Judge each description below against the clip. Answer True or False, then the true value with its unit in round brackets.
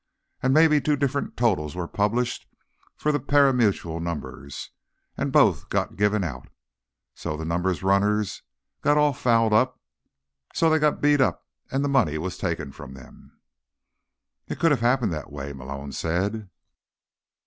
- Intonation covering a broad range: True (8.7 semitones)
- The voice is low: True (105 Hz)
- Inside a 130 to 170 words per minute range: True (150 wpm)